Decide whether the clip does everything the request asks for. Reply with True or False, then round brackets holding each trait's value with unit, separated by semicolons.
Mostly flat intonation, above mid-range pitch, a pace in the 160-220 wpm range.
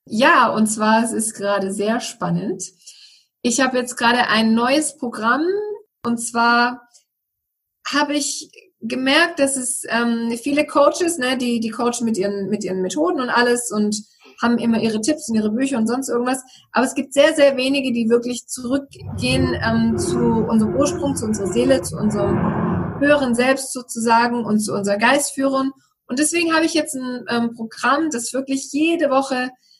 False (3.7 semitones; 240 Hz; 170 wpm)